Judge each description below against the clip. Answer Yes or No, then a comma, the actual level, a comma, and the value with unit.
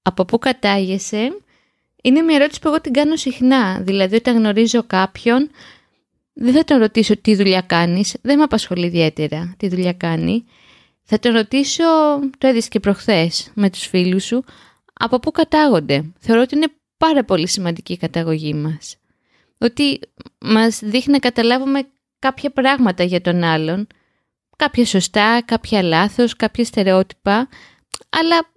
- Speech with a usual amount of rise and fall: No, wide, 6.0 semitones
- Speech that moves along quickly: No, average, 145 wpm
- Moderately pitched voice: No, high, 225 Hz